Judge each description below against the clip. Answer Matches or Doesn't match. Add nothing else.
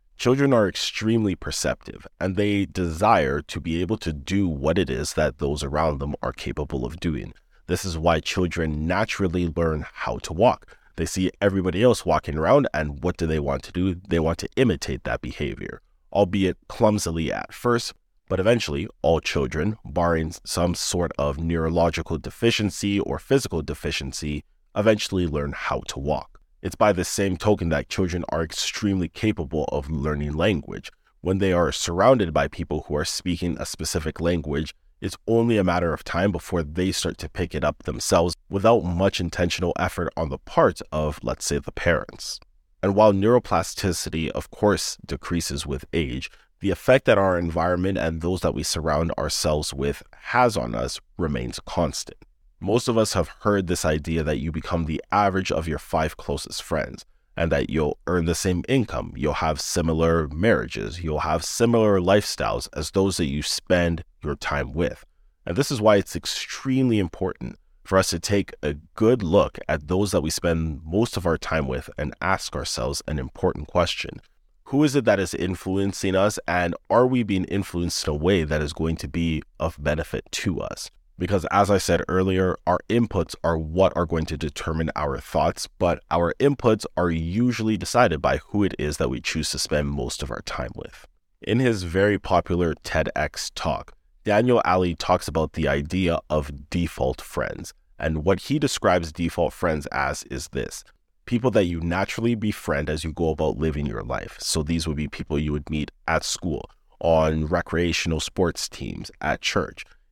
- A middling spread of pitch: Matches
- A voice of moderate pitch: Doesn't match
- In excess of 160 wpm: Matches